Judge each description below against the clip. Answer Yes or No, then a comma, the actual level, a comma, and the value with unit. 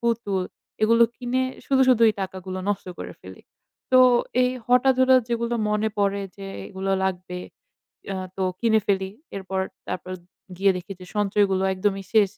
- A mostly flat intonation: No, average, 3.5 semitones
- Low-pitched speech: No, high, 200 Hz